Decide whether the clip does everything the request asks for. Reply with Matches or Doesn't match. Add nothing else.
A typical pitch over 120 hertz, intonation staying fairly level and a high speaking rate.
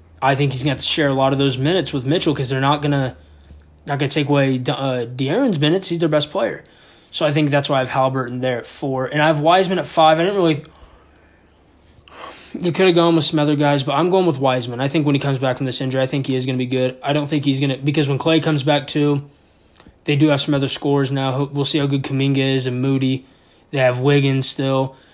Matches